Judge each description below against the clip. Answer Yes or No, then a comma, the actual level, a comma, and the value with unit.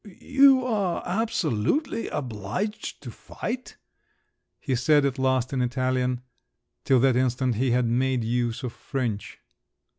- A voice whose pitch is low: Yes, low, 130 Hz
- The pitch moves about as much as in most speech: No, wide, 6.1 semitones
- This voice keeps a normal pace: No, slow, 125 wpm